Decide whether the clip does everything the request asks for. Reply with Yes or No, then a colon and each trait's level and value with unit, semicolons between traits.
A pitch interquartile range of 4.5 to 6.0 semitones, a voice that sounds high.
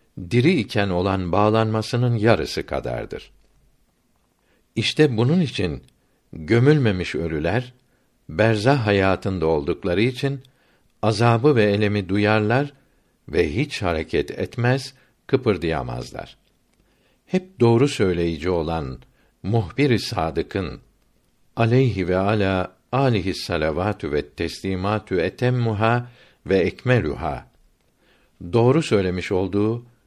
No: average, 5.0 semitones; low, 110 Hz